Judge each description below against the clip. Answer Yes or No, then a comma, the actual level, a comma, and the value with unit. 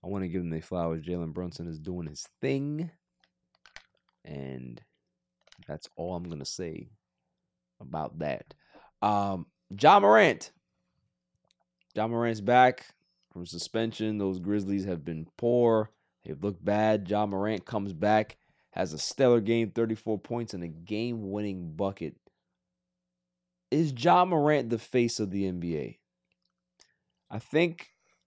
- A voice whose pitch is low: Yes, low, 100 Hz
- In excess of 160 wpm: No, slow, 135 wpm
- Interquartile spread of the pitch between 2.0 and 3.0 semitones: No, average, 5.1 semitones